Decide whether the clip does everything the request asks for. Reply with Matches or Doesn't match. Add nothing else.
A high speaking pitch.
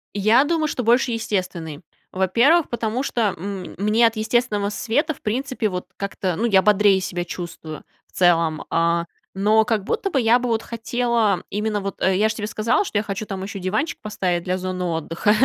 Matches